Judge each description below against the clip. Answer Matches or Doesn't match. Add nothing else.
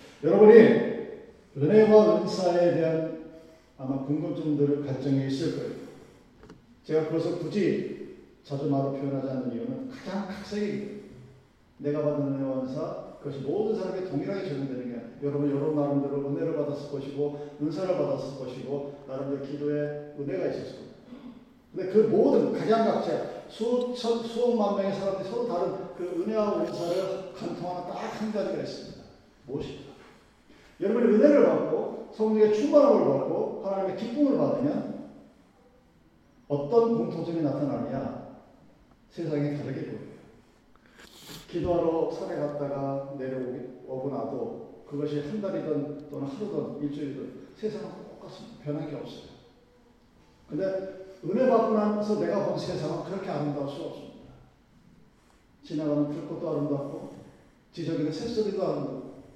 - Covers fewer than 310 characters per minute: Doesn't match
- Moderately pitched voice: Matches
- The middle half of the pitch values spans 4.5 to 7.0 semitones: Matches